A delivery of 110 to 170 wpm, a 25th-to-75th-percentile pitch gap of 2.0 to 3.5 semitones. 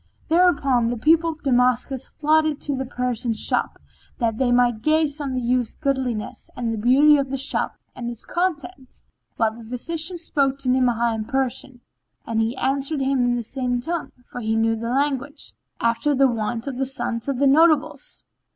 No: average, 185 wpm; average, 3.2 semitones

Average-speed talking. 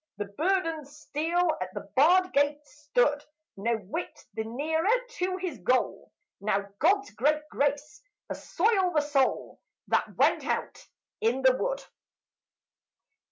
No: slow, 125 wpm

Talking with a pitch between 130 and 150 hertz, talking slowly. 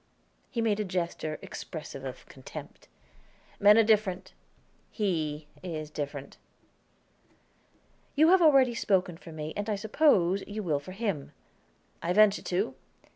No: medium, 185 Hz; slow, 130 wpm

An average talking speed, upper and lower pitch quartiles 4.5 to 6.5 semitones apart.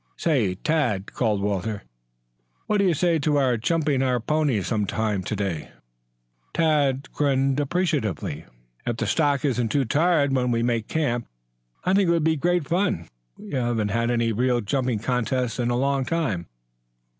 Yes: average, 170 wpm; average, 5.2 semitones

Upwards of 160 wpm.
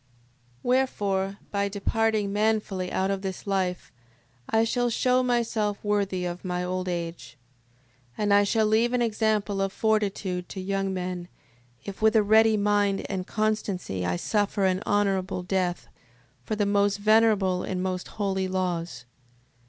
No: average, 150 wpm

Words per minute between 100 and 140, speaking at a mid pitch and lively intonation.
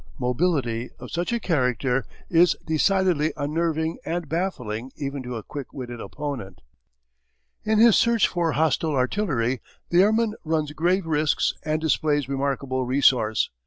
No: slow, 135 wpm; medium, 150 Hz; average, 4.9 semitones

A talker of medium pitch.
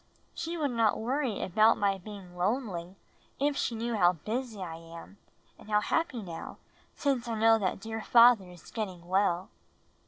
No: high, 215 Hz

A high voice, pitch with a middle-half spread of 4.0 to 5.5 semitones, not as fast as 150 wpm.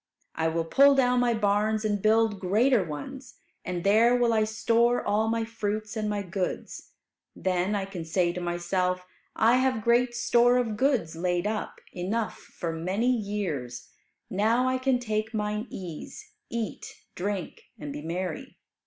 No: high, 210 Hz; average, 4.4 semitones; average, 160 wpm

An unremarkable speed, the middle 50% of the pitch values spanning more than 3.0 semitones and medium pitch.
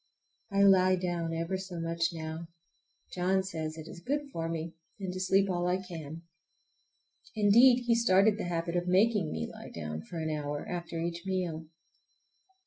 No: average, 170 wpm; average, 2.7 semitones; medium, 175 Hz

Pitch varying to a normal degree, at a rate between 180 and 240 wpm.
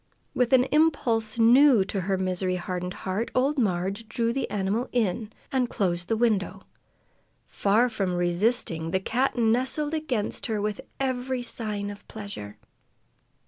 No: average, 4.6 semitones; average, 140 wpm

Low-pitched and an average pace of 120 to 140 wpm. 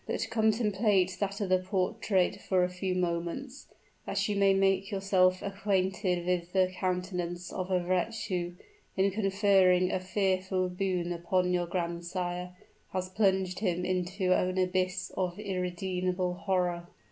No: medium, 185 Hz; slow, 135 wpm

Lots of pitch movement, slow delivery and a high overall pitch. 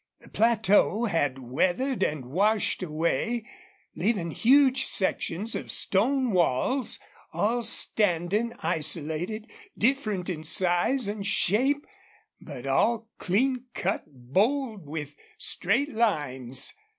Yes: wide, 6.7 semitones; slow, 100 wpm; high, 200 Hz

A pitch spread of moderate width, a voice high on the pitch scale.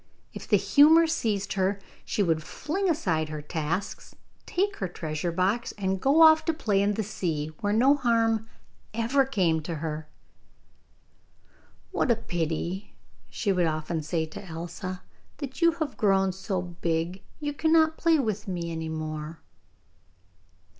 No: wide, 7.9 semitones; high, 195 Hz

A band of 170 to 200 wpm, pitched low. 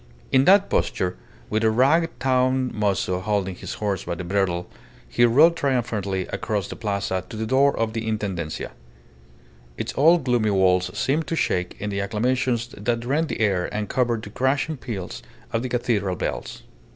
Yes: average, 175 wpm; low, 110 Hz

